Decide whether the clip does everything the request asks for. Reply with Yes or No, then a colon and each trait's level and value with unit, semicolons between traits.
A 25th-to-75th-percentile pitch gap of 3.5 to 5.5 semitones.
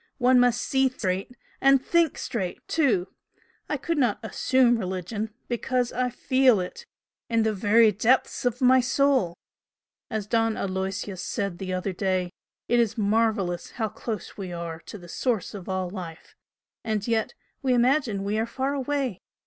Yes: average, 4.8 semitones